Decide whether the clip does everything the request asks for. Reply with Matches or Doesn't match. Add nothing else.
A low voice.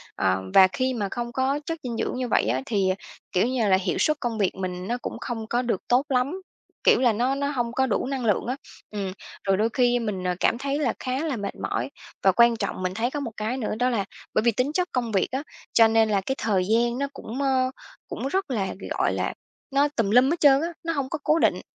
Doesn't match